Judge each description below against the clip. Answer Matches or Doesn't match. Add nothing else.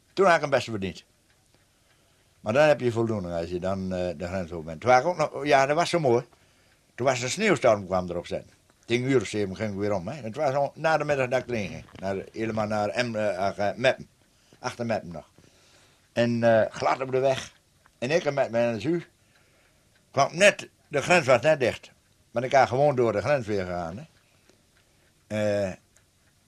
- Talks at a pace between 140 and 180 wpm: Doesn't match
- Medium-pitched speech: Doesn't match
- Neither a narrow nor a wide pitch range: Matches